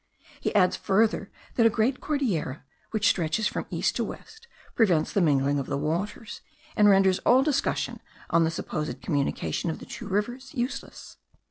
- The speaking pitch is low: No, high, 195 Hz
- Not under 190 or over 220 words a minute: No, average, 165 wpm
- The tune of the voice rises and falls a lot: Yes, wide, 6.3 semitones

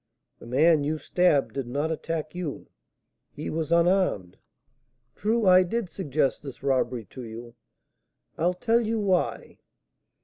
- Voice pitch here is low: No, medium, 160 Hz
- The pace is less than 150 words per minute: Yes, slow, 135 wpm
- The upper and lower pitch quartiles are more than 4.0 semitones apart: Yes, average, 5.0 semitones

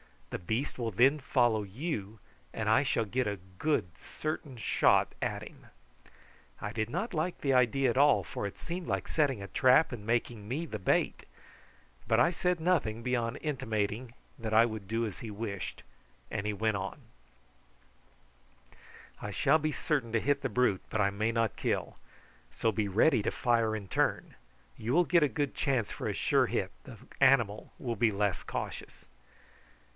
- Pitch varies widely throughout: No, average, 4.6 semitones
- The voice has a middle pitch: No, low, 115 Hz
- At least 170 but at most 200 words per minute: Yes, average, 180 wpm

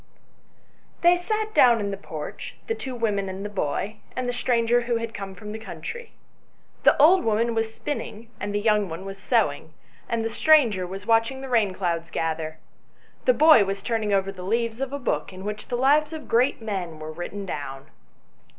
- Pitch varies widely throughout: No, average, 4.1 semitones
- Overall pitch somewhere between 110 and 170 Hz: No, high, 220 Hz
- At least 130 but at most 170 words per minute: No, average, 200 wpm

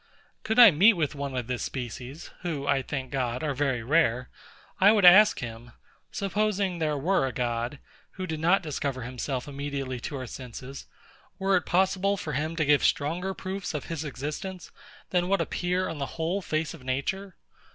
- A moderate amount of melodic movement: No, wide, 5.9 semitones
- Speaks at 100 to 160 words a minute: No, average, 185 wpm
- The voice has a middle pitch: Yes, medium, 150 Hz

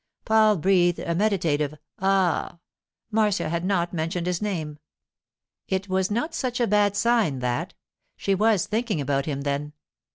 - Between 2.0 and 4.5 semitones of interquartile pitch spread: No, average, 4.9 semitones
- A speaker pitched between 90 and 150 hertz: No, medium, 185 Hz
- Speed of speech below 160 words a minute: Yes, average, 150 wpm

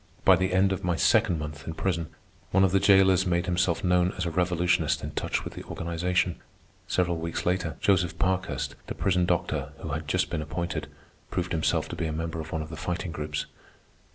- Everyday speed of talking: No, fast, 210 wpm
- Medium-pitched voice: No, very low, 90 Hz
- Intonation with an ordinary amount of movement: No, narrow, 2.1 semitones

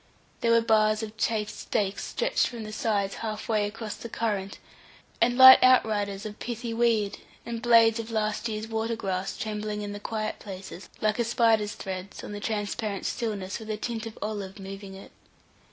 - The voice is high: Yes, high, 215 Hz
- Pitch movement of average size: No, narrow, 1.8 semitones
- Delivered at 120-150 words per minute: No, average, 185 wpm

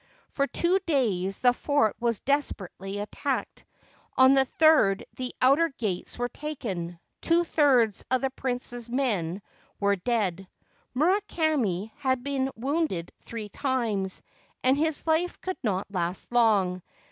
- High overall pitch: Yes, high, 245 Hz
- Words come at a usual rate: No, slow, 130 wpm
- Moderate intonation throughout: No, wide, 6.2 semitones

